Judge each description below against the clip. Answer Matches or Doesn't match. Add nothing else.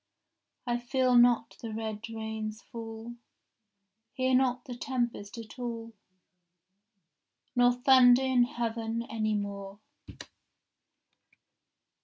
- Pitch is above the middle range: Matches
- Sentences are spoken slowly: Matches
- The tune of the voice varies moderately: Doesn't match